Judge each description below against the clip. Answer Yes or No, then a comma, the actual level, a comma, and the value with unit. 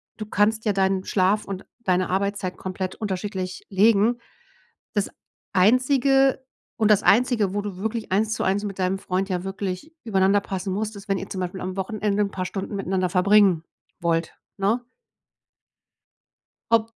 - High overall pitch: Yes, high, 195 Hz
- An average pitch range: No, narrow, 2.3 semitones